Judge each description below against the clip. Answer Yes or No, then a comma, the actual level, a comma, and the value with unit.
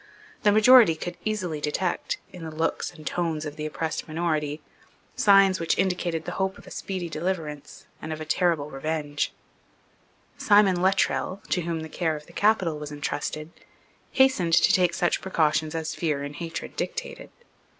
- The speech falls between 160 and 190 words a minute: Yes, average, 165 wpm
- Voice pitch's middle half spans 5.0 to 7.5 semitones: No, average, 3.4 semitones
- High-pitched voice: No, medium, 165 Hz